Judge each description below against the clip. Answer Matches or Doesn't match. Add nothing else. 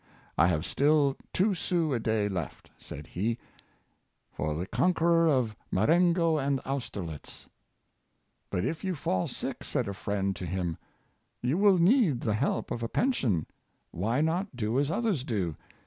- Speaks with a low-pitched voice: Matches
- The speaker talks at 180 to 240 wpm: Doesn't match